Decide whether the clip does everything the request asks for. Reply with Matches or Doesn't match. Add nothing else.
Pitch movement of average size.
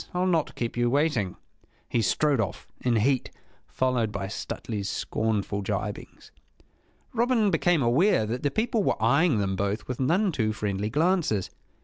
Doesn't match